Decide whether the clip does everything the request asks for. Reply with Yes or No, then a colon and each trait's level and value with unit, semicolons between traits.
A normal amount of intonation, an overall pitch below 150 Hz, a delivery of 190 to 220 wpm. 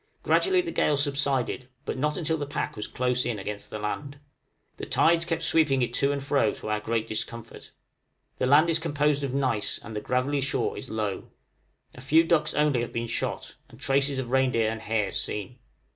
Yes: average, 4.1 semitones; low, 135 Hz; average, 200 wpm